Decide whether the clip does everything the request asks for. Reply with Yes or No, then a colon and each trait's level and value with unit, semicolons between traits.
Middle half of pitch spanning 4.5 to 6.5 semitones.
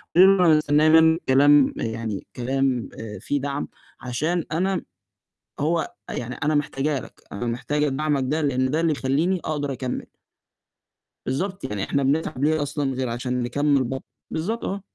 No: average, 3.3 semitones